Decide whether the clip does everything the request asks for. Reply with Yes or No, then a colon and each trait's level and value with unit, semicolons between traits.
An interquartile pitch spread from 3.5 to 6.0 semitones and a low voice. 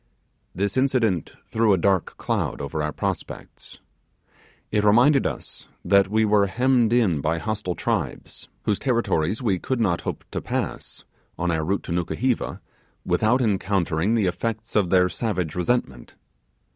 Yes: average, 4.5 semitones; low, 100 Hz